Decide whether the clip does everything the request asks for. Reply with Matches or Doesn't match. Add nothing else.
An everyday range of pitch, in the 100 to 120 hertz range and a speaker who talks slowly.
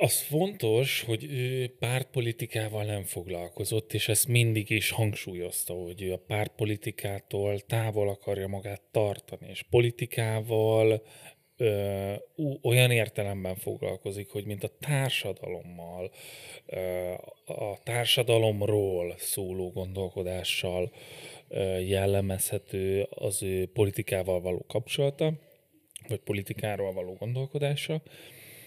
Matches